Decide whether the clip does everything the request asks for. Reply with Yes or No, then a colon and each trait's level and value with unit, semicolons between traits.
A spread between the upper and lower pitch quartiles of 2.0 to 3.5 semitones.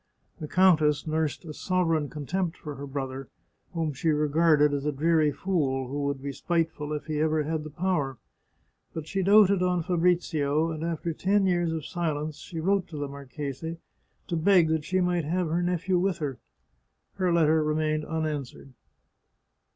Yes: average, 2.9 semitones